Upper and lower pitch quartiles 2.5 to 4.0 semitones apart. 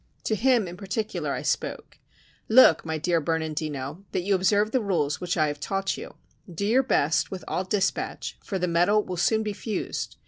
No: average, 4.6 semitones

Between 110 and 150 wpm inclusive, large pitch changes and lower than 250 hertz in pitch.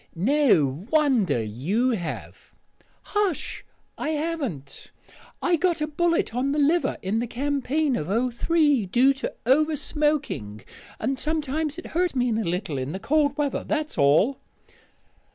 No: average, 145 wpm; wide, 7.4 semitones; very high, 275 Hz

